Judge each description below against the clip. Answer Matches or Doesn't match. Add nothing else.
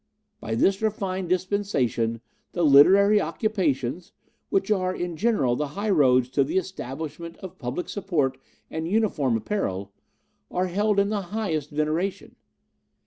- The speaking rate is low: Matches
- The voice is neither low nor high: Matches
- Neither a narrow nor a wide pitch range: Doesn't match